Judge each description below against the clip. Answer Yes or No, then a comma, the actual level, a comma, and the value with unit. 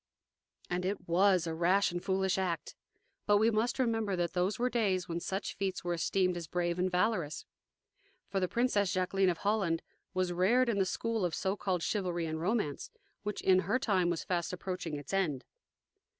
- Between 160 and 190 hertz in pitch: Yes, medium, 185 Hz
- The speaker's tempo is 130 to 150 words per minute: No, average, 190 wpm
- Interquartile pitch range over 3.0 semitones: No, average, 2.7 semitones